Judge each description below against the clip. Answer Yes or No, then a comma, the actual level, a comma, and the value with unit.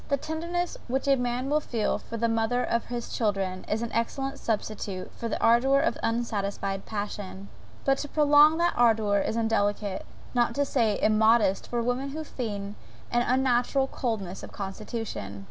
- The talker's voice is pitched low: No, high, 230 Hz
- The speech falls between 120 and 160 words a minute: No, average, 170 wpm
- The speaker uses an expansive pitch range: No, average, 4.4 semitones